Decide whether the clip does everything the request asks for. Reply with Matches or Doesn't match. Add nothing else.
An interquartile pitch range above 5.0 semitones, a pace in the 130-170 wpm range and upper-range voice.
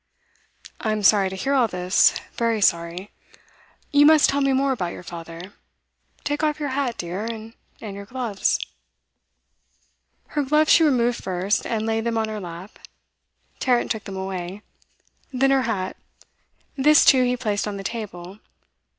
Matches